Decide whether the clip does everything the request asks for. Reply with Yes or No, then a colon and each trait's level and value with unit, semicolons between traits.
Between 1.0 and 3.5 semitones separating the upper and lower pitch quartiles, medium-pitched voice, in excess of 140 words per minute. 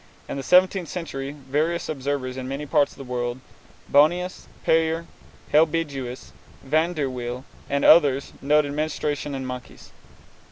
No: average, 3.2 semitones; medium, 145 Hz; slow, 135 wpm